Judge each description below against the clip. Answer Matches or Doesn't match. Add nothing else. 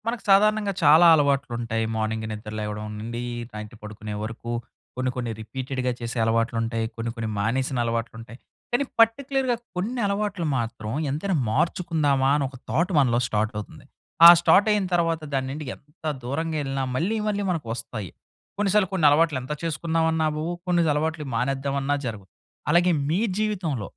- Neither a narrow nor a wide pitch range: Doesn't match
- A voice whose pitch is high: Doesn't match